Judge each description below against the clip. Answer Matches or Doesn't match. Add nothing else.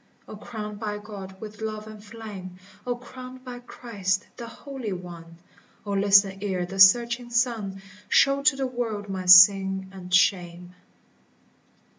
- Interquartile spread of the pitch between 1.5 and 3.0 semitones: Doesn't match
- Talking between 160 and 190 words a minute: Doesn't match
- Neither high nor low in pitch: Doesn't match